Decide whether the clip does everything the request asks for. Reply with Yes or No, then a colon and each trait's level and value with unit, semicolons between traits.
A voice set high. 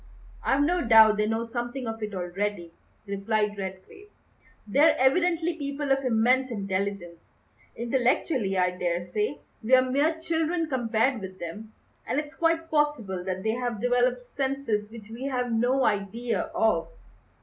Yes: high, 235 Hz